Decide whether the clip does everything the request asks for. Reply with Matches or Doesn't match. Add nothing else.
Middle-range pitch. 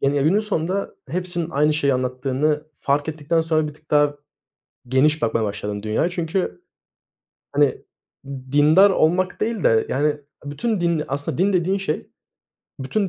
Matches